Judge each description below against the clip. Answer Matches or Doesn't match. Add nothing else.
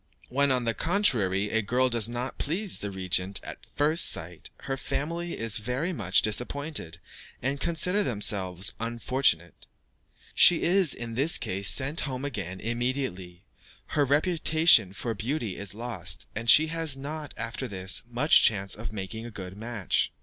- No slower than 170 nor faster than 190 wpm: Doesn't match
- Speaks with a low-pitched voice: Matches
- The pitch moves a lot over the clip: Matches